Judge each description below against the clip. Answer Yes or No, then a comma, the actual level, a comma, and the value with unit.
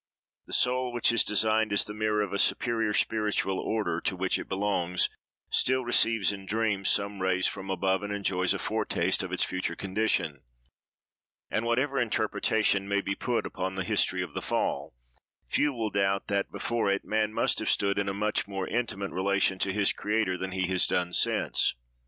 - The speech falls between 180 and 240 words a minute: Yes, average, 190 wpm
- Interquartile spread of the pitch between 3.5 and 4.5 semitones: No, narrow, 2.5 semitones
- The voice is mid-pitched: No, low, 100 Hz